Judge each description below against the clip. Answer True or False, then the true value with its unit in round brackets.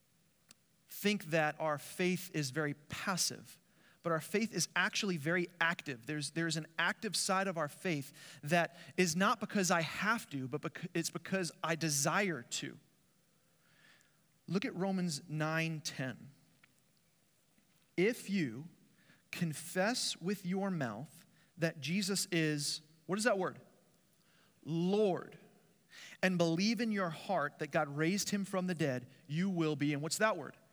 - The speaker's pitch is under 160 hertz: False (170 Hz)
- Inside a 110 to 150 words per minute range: True (145 wpm)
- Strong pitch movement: False (3.2 semitones)